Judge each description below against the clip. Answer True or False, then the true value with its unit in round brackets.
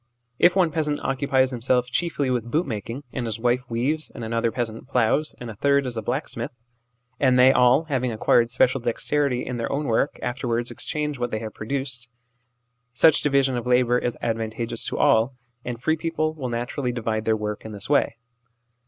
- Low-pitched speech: True (125 Hz)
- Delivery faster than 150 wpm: True (190 wpm)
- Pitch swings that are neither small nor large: True (3.3 semitones)